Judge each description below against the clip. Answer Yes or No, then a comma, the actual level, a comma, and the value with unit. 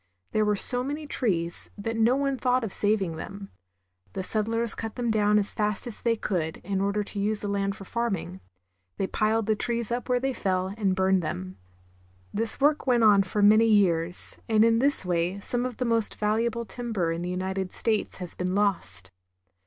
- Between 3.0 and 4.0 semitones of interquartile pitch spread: Yes, average, 3.4 semitones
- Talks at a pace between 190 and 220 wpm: Yes, average, 200 wpm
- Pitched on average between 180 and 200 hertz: No, high, 210 Hz